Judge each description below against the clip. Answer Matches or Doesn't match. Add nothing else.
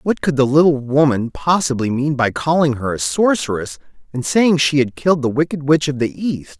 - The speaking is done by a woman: Doesn't match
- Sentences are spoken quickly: Matches